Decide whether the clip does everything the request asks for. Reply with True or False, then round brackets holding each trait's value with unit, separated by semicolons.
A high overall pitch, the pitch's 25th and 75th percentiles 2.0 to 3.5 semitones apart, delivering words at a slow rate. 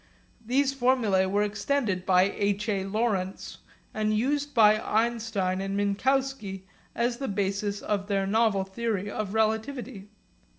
True (210 Hz; 3.2 semitones; 130 wpm)